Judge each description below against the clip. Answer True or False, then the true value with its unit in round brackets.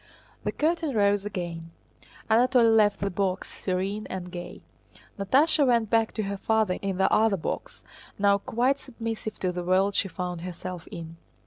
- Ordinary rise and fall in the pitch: True (3.6 semitones)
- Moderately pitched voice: False (200 Hz)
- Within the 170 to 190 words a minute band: False (160 wpm)